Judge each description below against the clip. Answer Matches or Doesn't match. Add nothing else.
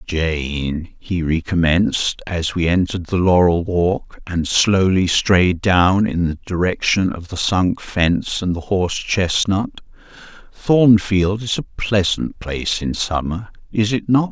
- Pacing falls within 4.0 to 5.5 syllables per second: Doesn't match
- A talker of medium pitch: Doesn't match